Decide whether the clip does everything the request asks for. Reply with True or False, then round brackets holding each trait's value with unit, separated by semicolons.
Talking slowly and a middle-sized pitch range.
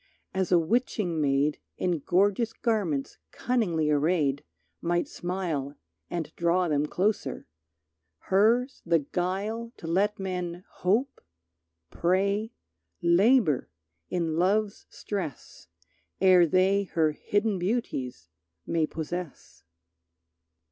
True (100 wpm; 4.0 semitones)